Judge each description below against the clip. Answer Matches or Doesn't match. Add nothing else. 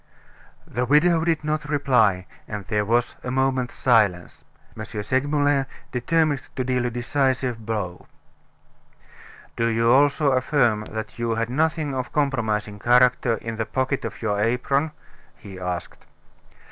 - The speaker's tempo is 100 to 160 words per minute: Matches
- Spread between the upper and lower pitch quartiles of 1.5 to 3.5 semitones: Doesn't match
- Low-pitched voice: Matches